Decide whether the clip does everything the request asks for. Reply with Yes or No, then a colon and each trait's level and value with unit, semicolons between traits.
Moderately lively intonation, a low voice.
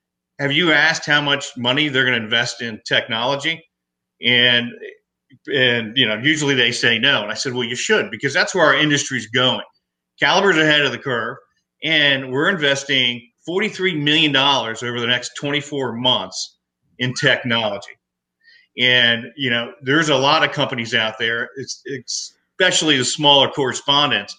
Yes: average, 3.4 semitones; low, 130 Hz